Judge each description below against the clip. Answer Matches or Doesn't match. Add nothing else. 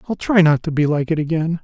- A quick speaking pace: Matches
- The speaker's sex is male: Matches